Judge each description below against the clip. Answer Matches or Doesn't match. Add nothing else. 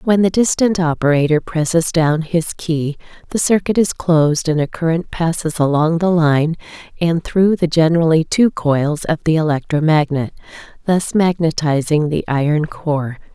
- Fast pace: Doesn't match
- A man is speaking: Doesn't match